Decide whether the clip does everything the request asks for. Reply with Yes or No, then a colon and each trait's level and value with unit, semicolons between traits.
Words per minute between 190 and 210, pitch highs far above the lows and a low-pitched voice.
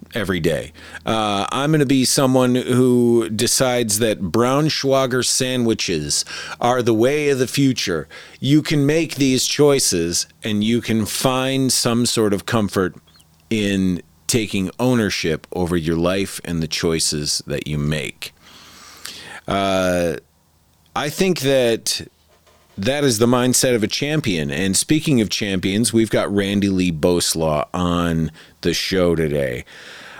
No: slow, 135 wpm; wide, 6.5 semitones; low, 110 Hz